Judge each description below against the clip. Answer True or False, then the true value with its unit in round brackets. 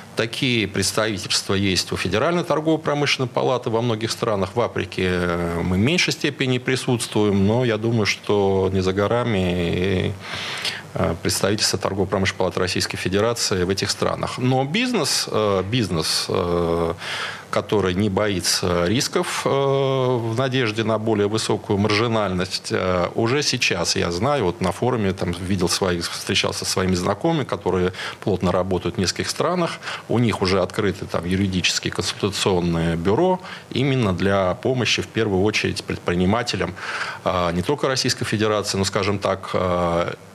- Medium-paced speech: True (130 wpm)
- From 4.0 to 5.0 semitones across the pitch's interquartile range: True (4.6 semitones)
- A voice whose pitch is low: True (100 Hz)